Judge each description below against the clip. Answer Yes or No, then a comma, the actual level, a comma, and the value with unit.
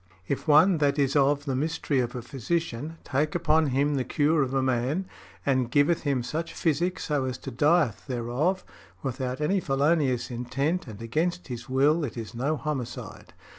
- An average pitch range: Yes, average, 3.5 semitones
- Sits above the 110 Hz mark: Yes, medium, 140 Hz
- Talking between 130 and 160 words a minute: No, average, 175 wpm